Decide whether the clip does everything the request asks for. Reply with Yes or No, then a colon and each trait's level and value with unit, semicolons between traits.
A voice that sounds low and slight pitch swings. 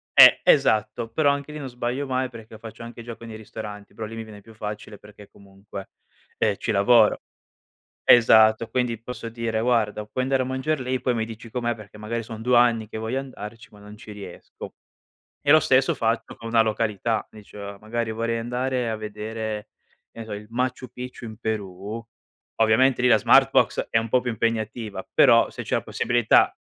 Yes: low, 115 Hz; narrow, 2.3 semitones